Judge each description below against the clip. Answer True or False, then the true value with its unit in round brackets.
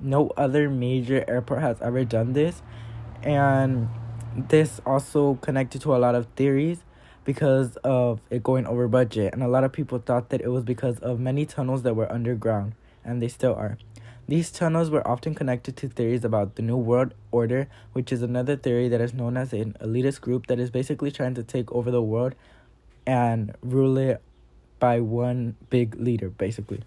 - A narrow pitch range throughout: True (2.3 semitones)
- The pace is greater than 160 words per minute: True (185 wpm)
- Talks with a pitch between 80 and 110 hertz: False (125 Hz)